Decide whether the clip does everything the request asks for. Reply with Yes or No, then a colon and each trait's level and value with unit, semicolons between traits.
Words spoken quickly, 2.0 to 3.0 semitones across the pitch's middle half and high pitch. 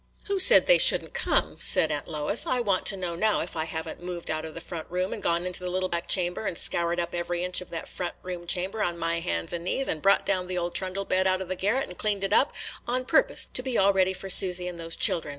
No: fast, 280 wpm; narrow, 2.4 semitones; medium, 180 Hz